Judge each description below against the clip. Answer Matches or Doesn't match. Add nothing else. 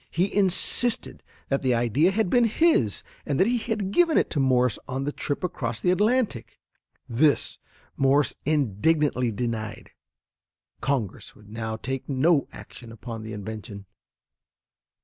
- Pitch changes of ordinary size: Doesn't match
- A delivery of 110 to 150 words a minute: Matches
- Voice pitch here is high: Doesn't match